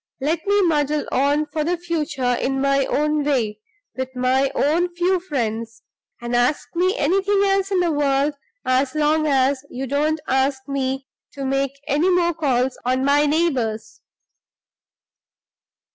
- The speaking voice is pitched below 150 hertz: No, very high, 285 Hz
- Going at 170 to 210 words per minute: No, average, 145 wpm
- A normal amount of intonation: Yes, average, 3.7 semitones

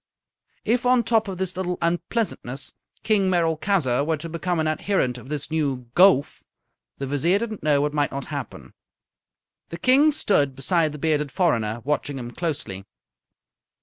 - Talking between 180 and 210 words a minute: No, average, 160 wpm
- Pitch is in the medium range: Yes, medium, 160 Hz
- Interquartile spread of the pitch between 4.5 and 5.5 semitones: Yes, average, 5.2 semitones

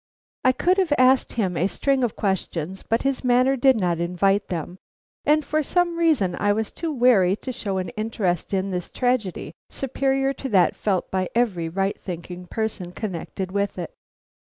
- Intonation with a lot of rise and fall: Yes, wide, 5.9 semitones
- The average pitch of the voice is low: No, high, 205 Hz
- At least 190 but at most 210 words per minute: No, average, 175 wpm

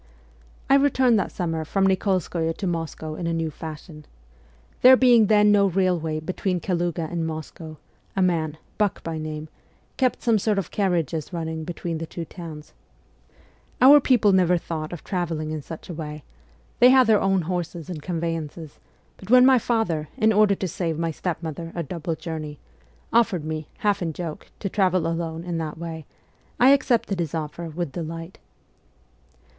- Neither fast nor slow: Yes, average, 175 wpm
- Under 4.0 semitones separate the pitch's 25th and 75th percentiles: Yes, average, 3.6 semitones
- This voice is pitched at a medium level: Yes, medium, 170 Hz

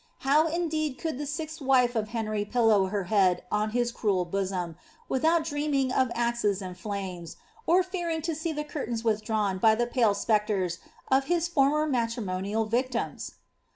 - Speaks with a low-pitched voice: No, high, 235 Hz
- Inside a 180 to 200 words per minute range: No, average, 165 wpm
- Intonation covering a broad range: Yes, wide, 6.4 semitones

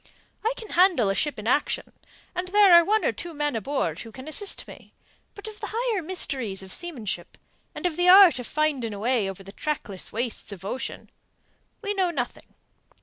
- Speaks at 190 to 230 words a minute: Yes, average, 200 wpm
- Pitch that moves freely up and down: Yes, wide, 8.4 semitones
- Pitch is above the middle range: Yes, very high, 295 Hz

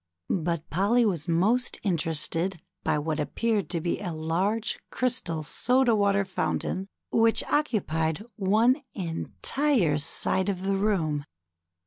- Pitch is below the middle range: No, high, 190 Hz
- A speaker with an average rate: No, slow, 120 wpm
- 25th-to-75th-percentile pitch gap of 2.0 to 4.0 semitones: No, average, 5.2 semitones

